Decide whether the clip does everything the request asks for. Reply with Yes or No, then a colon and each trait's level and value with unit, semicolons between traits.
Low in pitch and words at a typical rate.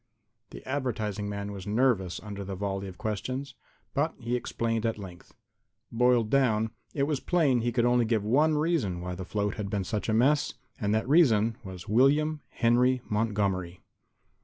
Yes: low, 110 Hz; average, 170 wpm